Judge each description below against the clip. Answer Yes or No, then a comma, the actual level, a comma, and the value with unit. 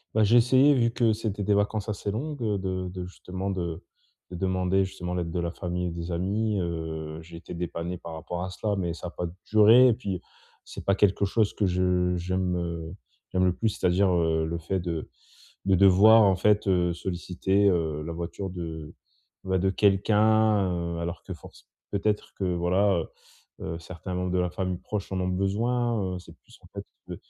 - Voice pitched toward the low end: Yes, very low, 95 Hz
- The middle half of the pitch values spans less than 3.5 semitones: Yes, average, 2.8 semitones